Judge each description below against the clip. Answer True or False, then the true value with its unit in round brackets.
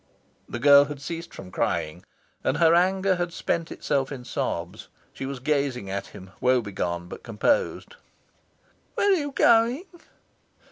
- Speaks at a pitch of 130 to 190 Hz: True (140 Hz)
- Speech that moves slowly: False (145 wpm)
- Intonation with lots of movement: True (8.3 semitones)